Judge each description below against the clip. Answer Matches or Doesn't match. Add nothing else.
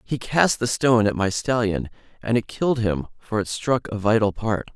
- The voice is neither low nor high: Doesn't match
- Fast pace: Matches